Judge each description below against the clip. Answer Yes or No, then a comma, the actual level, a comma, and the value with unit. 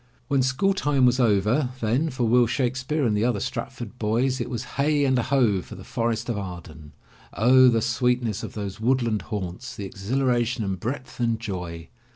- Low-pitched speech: Yes, low, 120 Hz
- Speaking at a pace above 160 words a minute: Yes, average, 190 wpm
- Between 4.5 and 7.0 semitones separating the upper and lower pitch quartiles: No, average, 3.5 semitones